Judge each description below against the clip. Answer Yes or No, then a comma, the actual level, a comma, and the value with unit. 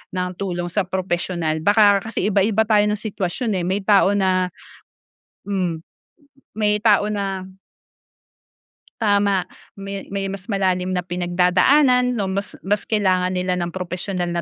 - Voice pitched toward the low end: No, high, 195 Hz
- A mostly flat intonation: Yes, narrow, 2.2 semitones